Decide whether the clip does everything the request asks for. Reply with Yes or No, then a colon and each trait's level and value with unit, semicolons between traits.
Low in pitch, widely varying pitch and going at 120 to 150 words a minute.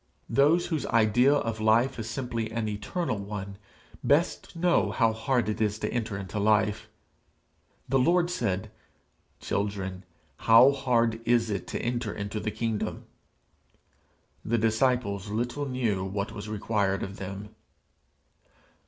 No: low, 110 Hz; average, 3.2 semitones; slow, 135 wpm